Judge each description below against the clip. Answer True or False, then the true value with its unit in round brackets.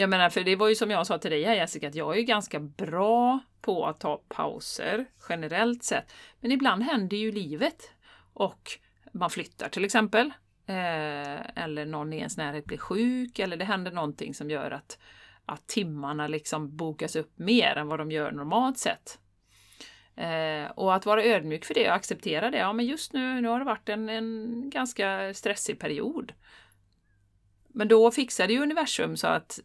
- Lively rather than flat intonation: True (6.6 semitones)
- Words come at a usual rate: True (180 wpm)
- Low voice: False (200 Hz)